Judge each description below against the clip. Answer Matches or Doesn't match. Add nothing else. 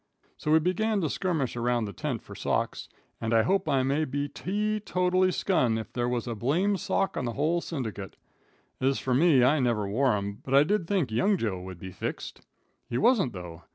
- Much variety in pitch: Matches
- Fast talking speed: Matches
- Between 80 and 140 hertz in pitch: Matches